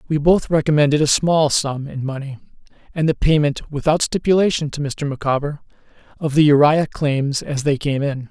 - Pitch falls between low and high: Yes, medium, 145 Hz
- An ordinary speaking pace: Yes, average, 175 wpm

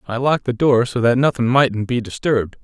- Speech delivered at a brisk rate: Yes, fast, 230 wpm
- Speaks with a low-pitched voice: Yes, low, 120 Hz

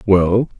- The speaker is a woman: No, male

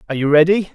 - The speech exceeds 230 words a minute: Yes, fast, 240 wpm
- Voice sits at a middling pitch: Yes, medium, 165 Hz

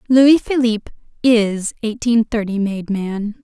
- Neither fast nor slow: No, slow, 120 wpm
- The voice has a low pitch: No, high, 225 Hz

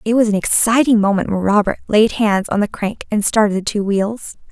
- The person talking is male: No, female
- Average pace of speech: No, fast, 225 wpm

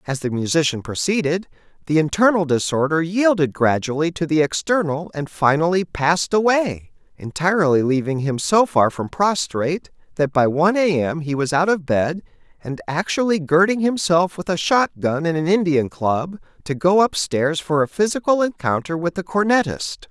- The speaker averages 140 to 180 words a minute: Yes, average, 165 wpm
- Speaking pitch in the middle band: Yes, medium, 165 Hz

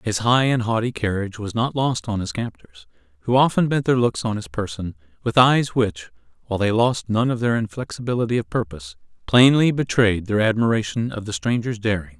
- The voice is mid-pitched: No, low, 110 Hz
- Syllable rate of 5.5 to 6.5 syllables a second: Yes, 5.6 syllables/s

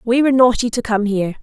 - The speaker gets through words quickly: Yes, fast, 255 wpm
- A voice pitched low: No, high, 230 Hz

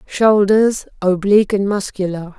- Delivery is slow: Yes, slow, 75 wpm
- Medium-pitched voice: No, high, 200 Hz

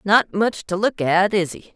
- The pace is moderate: No, fast, 240 wpm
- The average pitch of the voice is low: No, high, 190 Hz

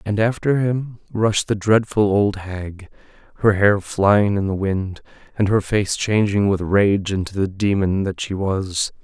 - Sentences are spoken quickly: No, average, 175 wpm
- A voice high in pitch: No, low, 100 Hz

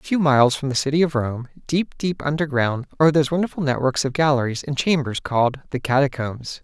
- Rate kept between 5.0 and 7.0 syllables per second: Yes, 6.0 syllables/s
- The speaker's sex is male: Yes, male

